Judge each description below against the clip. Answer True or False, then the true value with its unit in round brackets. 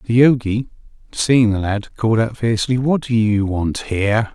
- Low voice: True (115 Hz)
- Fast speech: False (180 wpm)